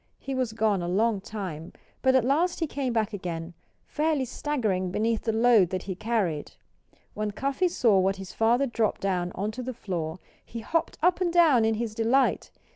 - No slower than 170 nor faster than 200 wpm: Yes, average, 190 wpm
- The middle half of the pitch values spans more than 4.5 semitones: Yes, average, 5.2 semitones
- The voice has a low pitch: No, high, 225 Hz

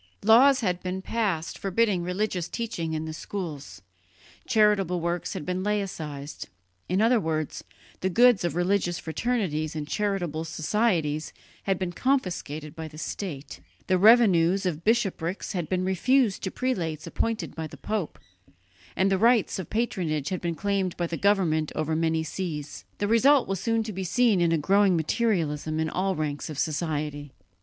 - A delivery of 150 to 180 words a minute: Yes, average, 160 wpm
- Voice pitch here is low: No, medium, 180 Hz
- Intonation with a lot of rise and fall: No, average, 4.6 semitones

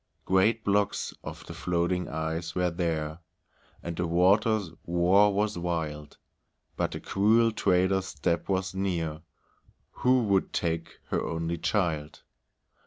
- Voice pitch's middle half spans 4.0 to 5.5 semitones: No, average, 3.1 semitones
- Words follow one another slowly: Yes, slow, 125 wpm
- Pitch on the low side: Yes, very low, 90 Hz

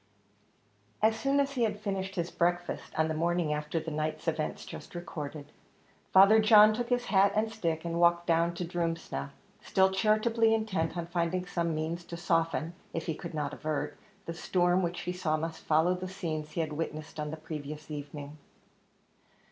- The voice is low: No, medium, 170 Hz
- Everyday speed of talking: Yes, average, 180 wpm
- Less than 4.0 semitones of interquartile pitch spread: Yes, average, 3.4 semitones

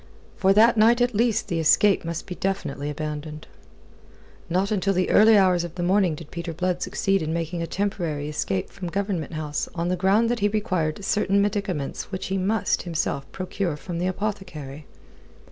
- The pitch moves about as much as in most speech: Yes, average, 3.8 semitones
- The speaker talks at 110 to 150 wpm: No, average, 180 wpm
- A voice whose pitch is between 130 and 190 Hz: Yes, medium, 185 Hz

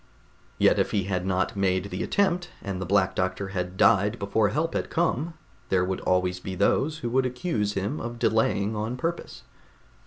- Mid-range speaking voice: No, low, 100 Hz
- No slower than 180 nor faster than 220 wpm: Yes, average, 185 wpm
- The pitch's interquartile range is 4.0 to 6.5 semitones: Yes, average, 5.1 semitones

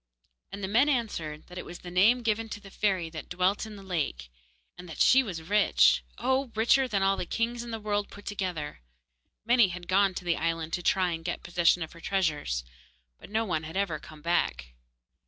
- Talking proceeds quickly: Yes, fast, 215 wpm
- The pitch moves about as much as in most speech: Yes, average, 4.3 semitones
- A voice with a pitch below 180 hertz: No, medium, 185 Hz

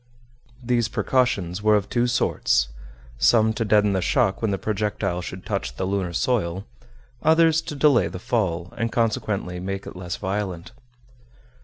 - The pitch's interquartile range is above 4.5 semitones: No, average, 4.1 semitones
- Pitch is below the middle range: Yes, low, 105 Hz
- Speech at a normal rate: Yes, average, 155 wpm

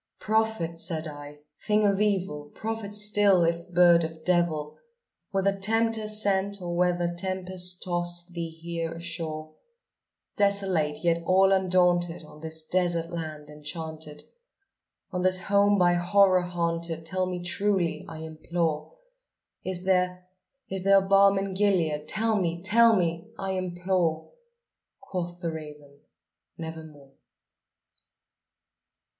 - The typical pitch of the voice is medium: Yes, medium, 175 Hz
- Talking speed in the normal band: No, slow, 120 wpm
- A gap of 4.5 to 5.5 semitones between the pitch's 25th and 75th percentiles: No, average, 2.8 semitones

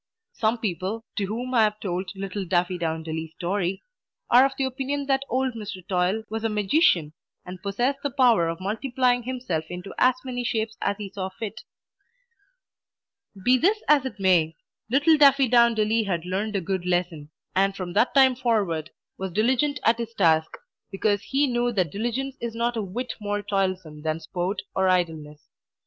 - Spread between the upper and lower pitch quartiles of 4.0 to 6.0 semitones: Yes, average, 5.2 semitones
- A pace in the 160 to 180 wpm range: Yes, average, 170 wpm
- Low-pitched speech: No, high, 205 Hz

